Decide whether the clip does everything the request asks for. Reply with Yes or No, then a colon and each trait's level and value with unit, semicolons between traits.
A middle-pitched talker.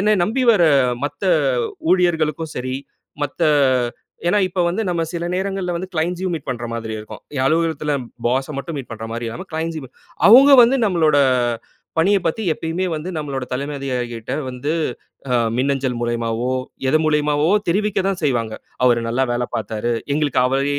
Yes: medium, 150 Hz